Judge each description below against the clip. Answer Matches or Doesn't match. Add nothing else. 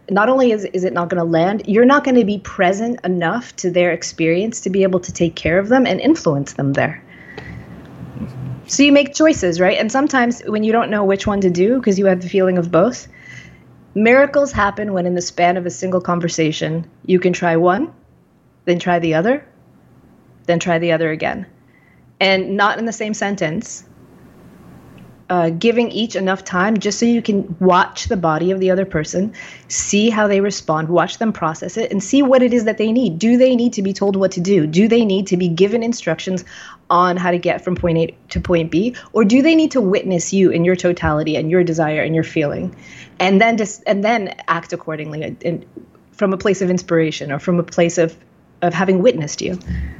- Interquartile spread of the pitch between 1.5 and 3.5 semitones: Doesn't match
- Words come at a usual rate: Doesn't match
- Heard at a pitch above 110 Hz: Matches